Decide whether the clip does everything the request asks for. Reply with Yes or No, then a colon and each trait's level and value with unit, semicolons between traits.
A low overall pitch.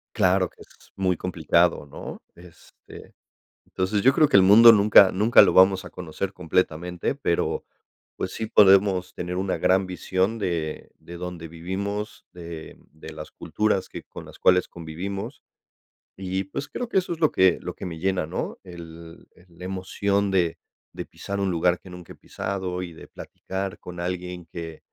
Yes: very low, 95 Hz